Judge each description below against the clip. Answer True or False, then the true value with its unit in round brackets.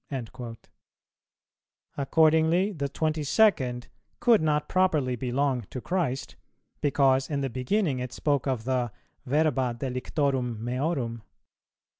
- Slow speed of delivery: True (110 wpm)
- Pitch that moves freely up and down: False (3.7 semitones)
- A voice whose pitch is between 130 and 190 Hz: True (135 Hz)